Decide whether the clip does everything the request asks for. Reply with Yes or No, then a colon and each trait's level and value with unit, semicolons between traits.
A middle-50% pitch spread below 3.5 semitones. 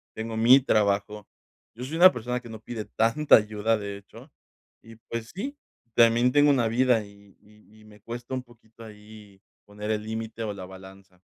Yes: narrow, 2.5 semitones